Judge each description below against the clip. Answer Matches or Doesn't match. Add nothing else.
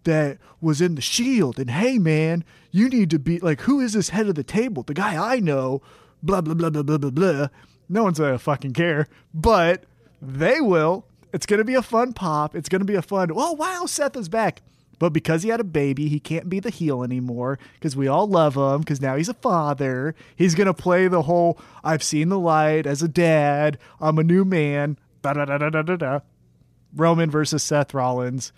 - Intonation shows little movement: Doesn't match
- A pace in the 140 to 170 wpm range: Doesn't match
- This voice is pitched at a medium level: Matches